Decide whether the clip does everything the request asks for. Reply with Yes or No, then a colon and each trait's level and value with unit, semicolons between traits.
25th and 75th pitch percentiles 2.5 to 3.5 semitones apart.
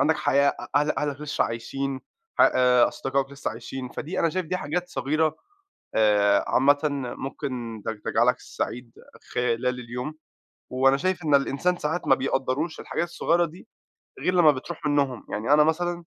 No: average, 3.9 semitones